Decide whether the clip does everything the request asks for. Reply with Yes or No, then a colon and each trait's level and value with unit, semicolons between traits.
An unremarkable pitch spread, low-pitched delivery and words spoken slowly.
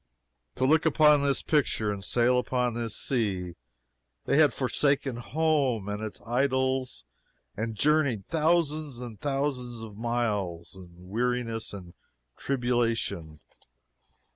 Yes: average, 4.5 semitones; low, 120 Hz; slow, 115 wpm